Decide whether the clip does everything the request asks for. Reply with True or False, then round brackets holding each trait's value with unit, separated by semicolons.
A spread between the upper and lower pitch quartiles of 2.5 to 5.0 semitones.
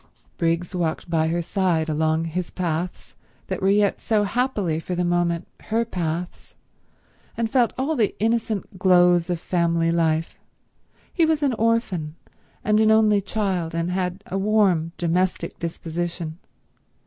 True (4.1 semitones)